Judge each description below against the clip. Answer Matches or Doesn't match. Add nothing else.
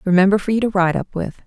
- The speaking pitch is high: Matches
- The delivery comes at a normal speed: Doesn't match